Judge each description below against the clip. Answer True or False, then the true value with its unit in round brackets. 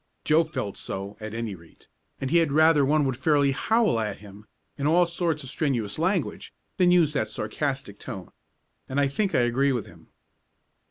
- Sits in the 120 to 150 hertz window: True (140 Hz)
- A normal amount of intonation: False (6.2 semitones)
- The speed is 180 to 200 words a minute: True (185 wpm)